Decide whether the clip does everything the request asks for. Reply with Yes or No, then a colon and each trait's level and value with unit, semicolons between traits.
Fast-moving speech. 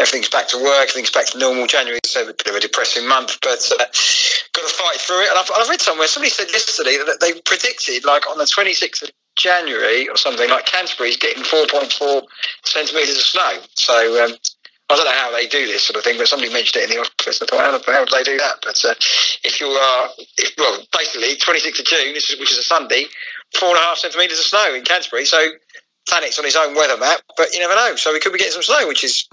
Yes: fast, 250 wpm